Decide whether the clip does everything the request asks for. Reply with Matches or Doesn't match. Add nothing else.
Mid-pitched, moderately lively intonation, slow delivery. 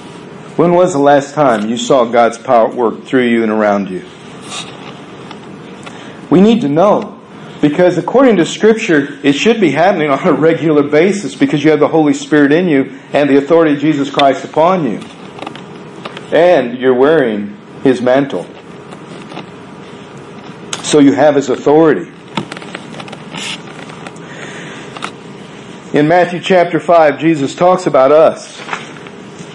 Matches